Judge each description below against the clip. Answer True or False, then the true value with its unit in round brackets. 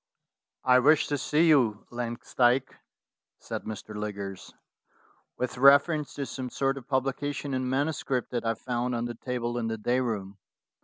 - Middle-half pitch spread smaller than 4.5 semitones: True (2.8 semitones)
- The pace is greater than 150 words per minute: True (160 wpm)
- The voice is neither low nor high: False (125 Hz)